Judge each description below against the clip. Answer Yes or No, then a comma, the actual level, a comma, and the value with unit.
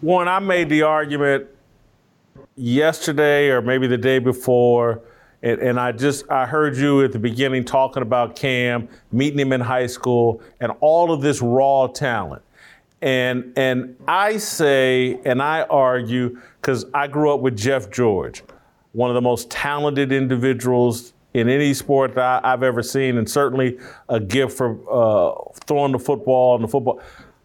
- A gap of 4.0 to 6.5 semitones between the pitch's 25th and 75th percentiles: No, narrow, 2.4 semitones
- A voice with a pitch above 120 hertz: Yes, low, 130 Hz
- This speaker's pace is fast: No, average, 165 wpm